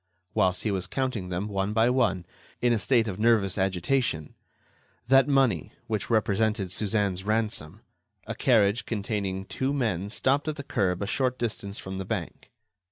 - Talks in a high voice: No, low, 105 Hz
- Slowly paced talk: No, average, 155 wpm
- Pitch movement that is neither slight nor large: Yes, average, 3.8 semitones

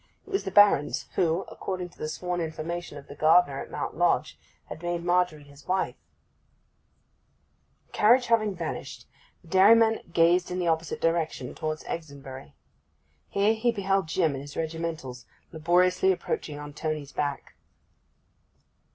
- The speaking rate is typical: Yes, average, 145 wpm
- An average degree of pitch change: Yes, average, 3.4 semitones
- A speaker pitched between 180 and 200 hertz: No, medium, 170 Hz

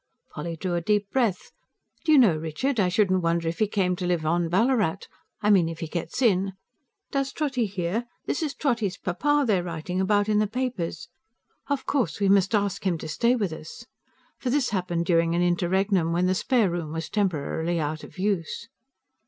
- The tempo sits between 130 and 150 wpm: No, average, 195 wpm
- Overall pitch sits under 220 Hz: Yes, high, 190 Hz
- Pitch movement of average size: Yes, average, 4.3 semitones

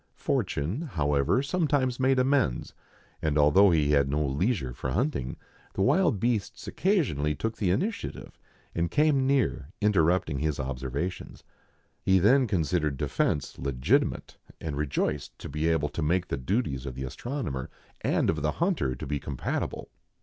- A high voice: No, very low, 80 Hz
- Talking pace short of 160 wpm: Yes, average, 150 wpm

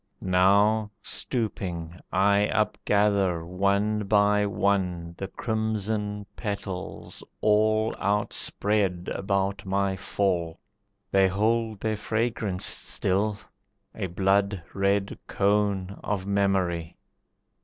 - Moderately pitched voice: No, low, 100 Hz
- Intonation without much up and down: Yes, narrow, 1.6 semitones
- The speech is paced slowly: Yes, slow, 90 wpm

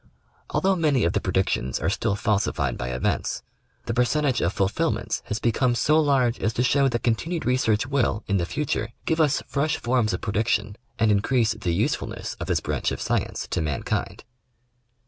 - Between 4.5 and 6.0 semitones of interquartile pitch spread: Yes, average, 5.1 semitones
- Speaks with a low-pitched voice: Yes, low, 115 Hz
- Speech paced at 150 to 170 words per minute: No, average, 185 wpm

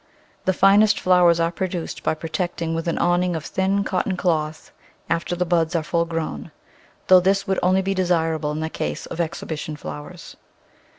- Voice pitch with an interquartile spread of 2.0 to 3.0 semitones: Yes, narrow, 2.4 semitones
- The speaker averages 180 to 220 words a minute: Yes, average, 185 wpm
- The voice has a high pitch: No, medium, 170 Hz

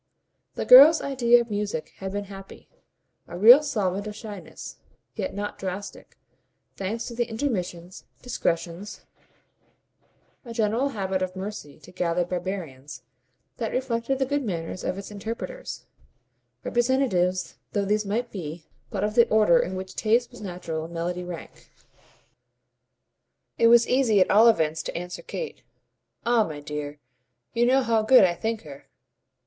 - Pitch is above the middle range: Yes, high, 205 Hz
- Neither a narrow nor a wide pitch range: Yes, average, 4.7 semitones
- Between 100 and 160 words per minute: Yes, average, 150 wpm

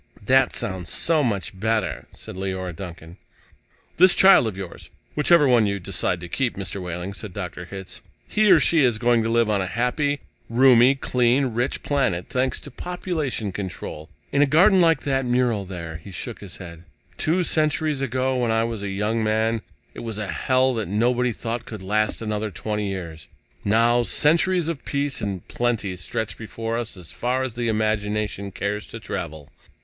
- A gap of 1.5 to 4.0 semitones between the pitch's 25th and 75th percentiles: No, average, 5.0 semitones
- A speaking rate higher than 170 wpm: Yes, average, 180 wpm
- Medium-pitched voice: No, low, 115 Hz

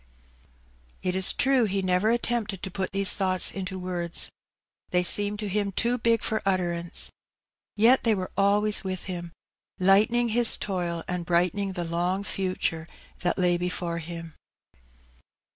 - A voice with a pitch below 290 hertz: Yes, high, 190 Hz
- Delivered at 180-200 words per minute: No, average, 145 wpm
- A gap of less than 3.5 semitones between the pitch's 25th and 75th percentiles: Yes, average, 2.8 semitones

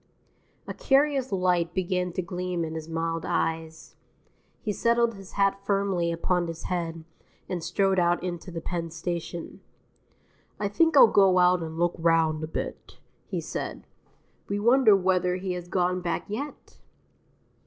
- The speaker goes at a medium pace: Yes, average, 155 wpm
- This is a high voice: No, medium, 180 Hz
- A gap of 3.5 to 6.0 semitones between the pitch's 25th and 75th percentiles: No, average, 2.9 semitones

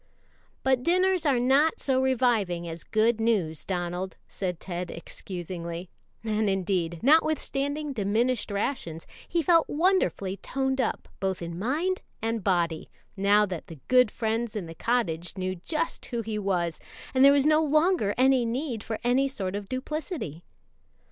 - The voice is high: Yes, high, 225 Hz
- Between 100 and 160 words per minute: Yes, average, 150 wpm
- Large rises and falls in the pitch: Yes, wide, 6.5 semitones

